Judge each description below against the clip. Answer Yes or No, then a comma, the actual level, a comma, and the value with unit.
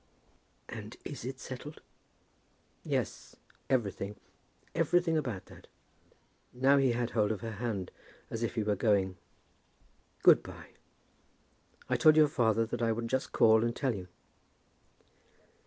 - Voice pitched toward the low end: Yes, low, 115 Hz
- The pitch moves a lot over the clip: No, average, 3.5 semitones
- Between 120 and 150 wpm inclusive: Yes, slow, 135 wpm